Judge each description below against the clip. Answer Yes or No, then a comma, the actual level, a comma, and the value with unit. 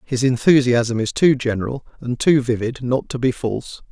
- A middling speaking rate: Yes, average, 185 wpm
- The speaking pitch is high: No, low, 125 Hz